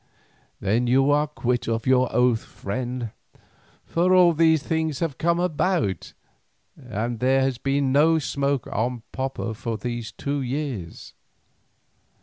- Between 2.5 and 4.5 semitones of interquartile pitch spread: Yes, average, 3.9 semitones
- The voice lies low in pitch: Yes, low, 130 Hz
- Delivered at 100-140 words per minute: Yes, slow, 135 wpm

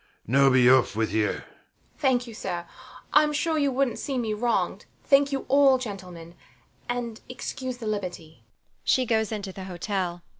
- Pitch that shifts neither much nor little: No, wide, 7.8 semitones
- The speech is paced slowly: No, average, 145 wpm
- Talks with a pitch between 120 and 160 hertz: No, high, 235 Hz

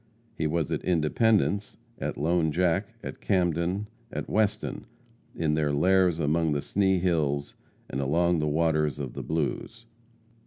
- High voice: No, very low, 85 Hz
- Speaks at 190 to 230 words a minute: No, average, 145 wpm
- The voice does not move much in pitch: No, average, 3.5 semitones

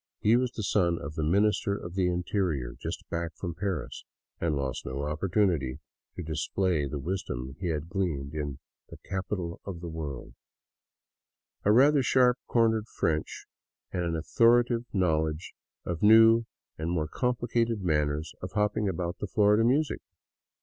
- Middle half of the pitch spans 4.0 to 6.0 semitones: Yes, average, 5.3 semitones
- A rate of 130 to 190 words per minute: Yes, average, 160 wpm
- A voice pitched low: Yes, very low, 90 Hz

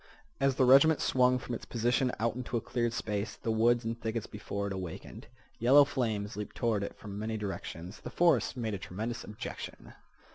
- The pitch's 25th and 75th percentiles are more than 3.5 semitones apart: No, average, 3.2 semitones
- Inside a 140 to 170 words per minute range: No, average, 190 wpm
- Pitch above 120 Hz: No, low, 115 Hz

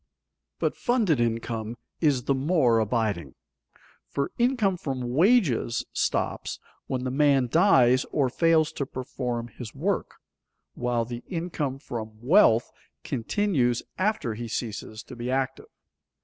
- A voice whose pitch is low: Yes, low, 130 Hz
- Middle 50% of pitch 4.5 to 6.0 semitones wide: Yes, wide, 5.4 semitones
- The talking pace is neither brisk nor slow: No, slow, 125 wpm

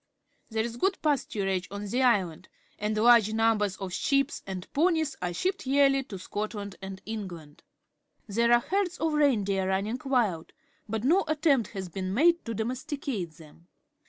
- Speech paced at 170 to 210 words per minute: No, average, 160 wpm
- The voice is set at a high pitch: Yes, high, 220 Hz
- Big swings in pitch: Yes, wide, 6.2 semitones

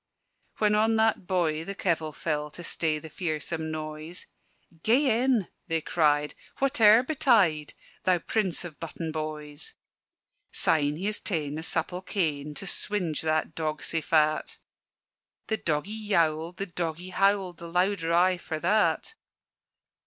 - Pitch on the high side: No, medium, 170 Hz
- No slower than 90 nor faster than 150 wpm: Yes, average, 140 wpm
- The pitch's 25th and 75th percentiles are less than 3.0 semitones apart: No, average, 4.2 semitones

